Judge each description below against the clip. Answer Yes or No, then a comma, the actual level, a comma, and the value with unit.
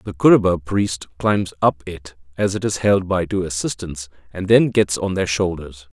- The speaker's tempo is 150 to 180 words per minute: No, average, 190 wpm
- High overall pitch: No, very low, 90 Hz